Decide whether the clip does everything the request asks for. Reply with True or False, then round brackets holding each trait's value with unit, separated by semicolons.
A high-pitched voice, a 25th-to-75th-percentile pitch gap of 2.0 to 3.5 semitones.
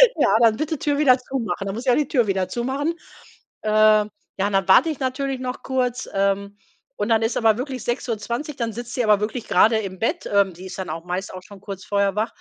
False (220 Hz; 4.3 semitones)